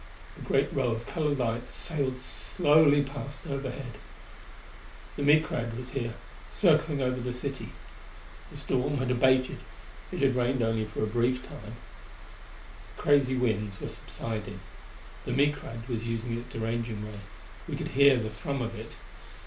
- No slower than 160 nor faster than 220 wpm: No, average, 150 wpm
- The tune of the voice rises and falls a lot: No, average, 3.3 semitones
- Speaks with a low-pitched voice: Yes, low, 125 Hz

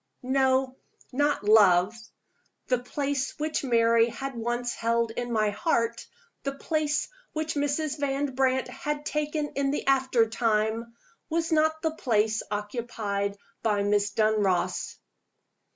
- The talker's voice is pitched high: Yes, high, 245 Hz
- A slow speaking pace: Yes, slow, 125 wpm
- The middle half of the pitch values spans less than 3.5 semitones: No, average, 4.7 semitones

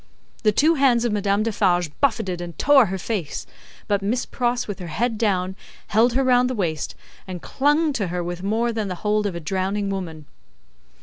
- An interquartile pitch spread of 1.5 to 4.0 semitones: No, average, 4.7 semitones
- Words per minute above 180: Yes, average, 195 wpm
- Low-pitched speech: No, high, 205 Hz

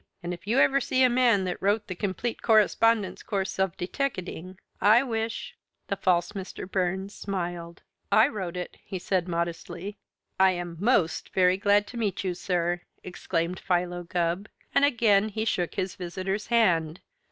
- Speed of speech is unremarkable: Yes, average, 165 wpm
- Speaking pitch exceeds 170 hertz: Yes, high, 190 Hz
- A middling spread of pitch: Yes, average, 3.5 semitones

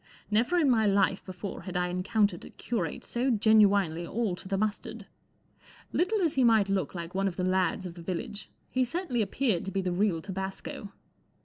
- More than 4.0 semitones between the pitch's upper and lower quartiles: No, average, 3.7 semitones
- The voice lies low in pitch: No, high, 200 Hz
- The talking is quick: No, average, 195 wpm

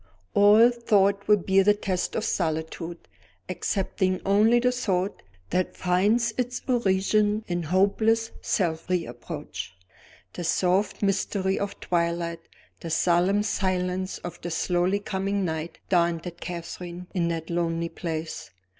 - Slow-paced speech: Yes, slow, 125 wpm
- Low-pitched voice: No, medium, 185 Hz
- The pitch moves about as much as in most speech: Yes, average, 3.1 semitones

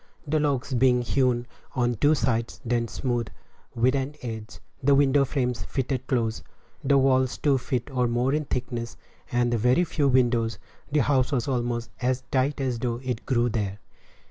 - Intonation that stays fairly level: Yes, narrow, 2.2 semitones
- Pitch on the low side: Yes, low, 125 Hz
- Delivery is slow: No, average, 170 wpm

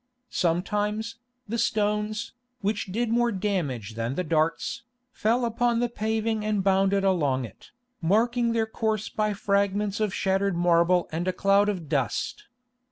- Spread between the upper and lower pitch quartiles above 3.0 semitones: Yes, average, 3.7 semitones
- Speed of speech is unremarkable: Yes, average, 145 wpm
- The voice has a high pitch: Yes, high, 205 Hz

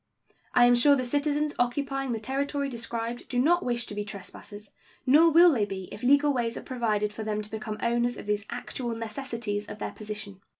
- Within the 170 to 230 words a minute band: Yes, fast, 205 wpm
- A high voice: Yes, high, 235 Hz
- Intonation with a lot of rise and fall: No, average, 4.3 semitones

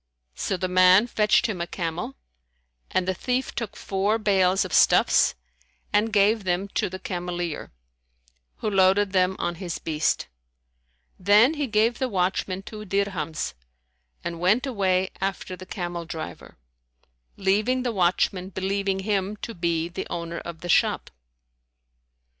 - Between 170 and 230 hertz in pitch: Yes, high, 190 Hz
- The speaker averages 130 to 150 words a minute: Yes, average, 140 wpm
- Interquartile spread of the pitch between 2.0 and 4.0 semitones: Yes, average, 2.8 semitones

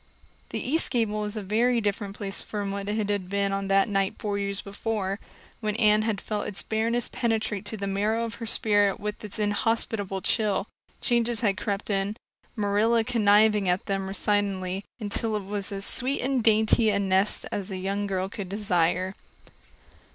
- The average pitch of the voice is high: Yes, high, 205 Hz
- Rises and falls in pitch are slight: Yes, narrow, 2.0 semitones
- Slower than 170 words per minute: No, average, 180 wpm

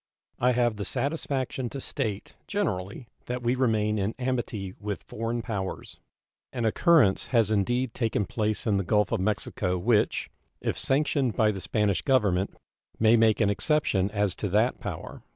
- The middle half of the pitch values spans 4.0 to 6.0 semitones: No, average, 3.5 semitones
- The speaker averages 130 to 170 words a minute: Yes, average, 160 wpm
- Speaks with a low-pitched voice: Yes, low, 110 Hz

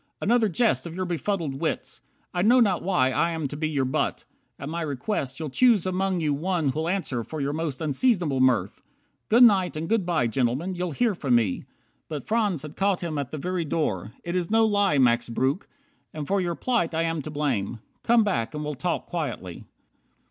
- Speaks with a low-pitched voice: No, medium, 165 Hz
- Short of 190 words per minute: No, fast, 205 wpm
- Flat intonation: No, average, 5.3 semitones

